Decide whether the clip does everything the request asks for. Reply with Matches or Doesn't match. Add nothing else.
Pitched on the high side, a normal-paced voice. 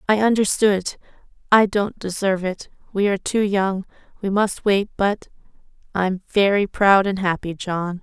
Doesn't match